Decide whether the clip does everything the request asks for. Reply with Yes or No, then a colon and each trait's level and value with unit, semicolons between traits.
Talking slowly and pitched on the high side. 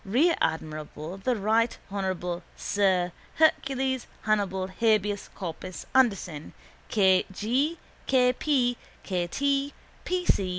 Yes: slow, 100 wpm; high, 210 Hz